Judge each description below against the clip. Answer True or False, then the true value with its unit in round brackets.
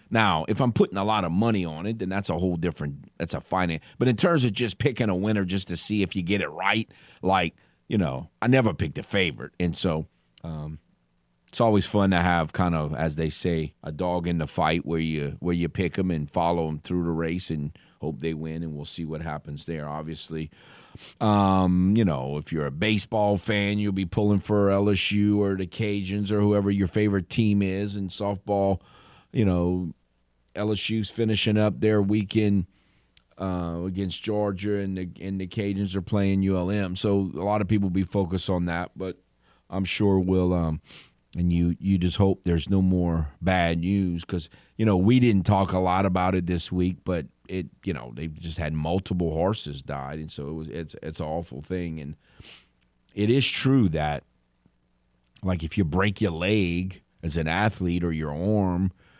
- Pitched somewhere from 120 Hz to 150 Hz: False (95 Hz)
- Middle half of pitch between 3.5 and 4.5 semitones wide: True (3.8 semitones)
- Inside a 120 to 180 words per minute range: False (200 wpm)